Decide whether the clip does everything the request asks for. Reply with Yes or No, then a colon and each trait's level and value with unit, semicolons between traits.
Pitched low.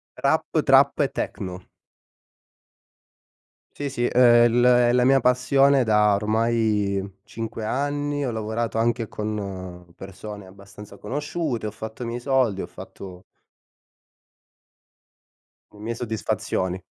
Yes: low, 110 Hz